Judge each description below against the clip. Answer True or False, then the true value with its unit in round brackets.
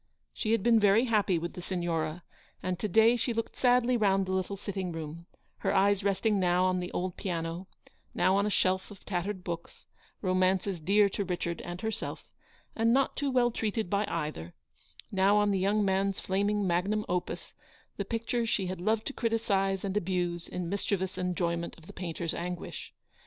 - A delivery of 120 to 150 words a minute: False (185 wpm)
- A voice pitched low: False (190 Hz)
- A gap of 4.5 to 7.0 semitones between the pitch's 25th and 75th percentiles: False (2.9 semitones)